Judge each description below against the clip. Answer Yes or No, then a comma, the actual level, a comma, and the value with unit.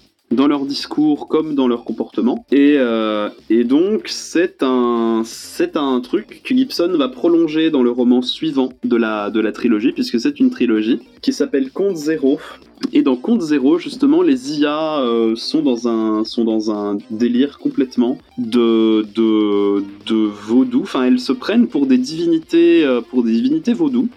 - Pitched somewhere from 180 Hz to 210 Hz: No, low, 135 Hz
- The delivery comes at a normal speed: Yes, average, 170 wpm